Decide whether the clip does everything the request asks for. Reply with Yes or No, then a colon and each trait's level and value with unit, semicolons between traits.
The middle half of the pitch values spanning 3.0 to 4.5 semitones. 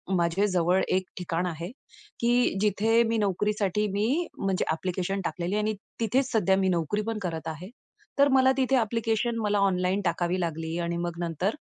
Yes: average, 4.1 semitones